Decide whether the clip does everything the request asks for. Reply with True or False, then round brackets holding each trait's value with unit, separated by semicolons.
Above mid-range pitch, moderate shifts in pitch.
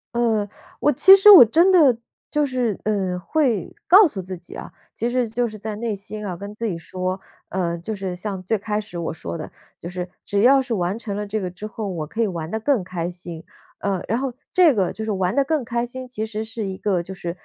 True (210 Hz; 4.5 semitones)